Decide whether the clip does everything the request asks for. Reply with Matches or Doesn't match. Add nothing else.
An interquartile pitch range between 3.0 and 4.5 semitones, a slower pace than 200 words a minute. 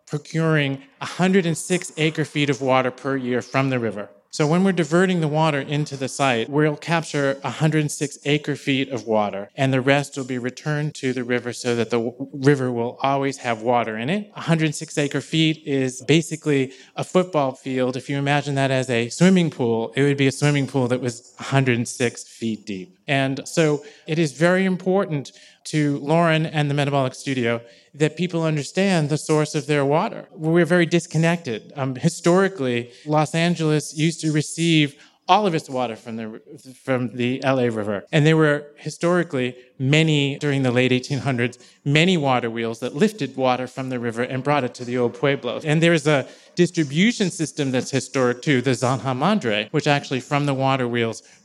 Matches